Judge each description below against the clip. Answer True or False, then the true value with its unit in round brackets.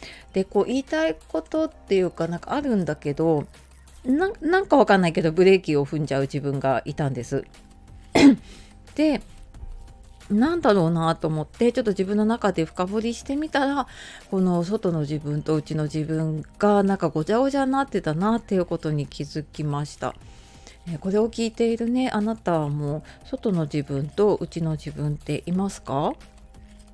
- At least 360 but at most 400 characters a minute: False (340 characters per minute)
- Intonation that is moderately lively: False (6.8 semitones)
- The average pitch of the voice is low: False (175 Hz)